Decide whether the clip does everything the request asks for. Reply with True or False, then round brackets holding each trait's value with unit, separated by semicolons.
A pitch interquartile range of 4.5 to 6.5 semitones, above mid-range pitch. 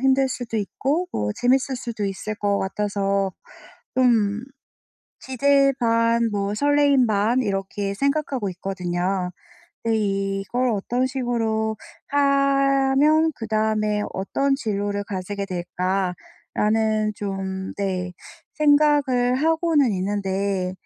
True (5.2 semitones; 220 Hz)